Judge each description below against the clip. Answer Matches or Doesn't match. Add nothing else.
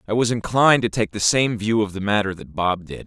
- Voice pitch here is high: Doesn't match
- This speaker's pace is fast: Matches